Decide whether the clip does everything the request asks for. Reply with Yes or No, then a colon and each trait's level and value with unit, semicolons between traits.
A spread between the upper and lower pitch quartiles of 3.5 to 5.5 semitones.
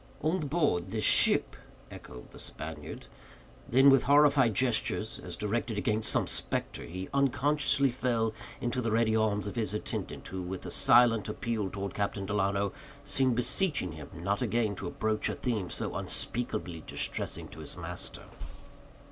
Yes: average, 4.3 semitones